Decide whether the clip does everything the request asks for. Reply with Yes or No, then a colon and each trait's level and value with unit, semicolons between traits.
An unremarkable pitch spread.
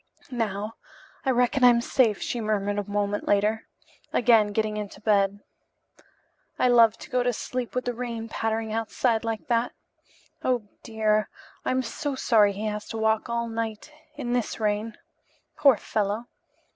No: narrow, 2.3 semitones